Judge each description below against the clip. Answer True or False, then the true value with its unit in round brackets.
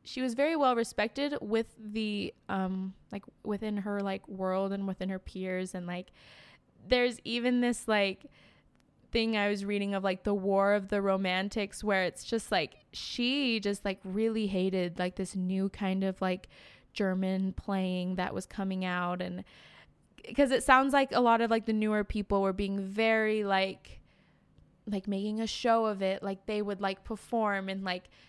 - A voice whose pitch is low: False (200 Hz)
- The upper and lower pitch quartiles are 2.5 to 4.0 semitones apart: True (2.8 semitones)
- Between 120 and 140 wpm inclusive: False (180 wpm)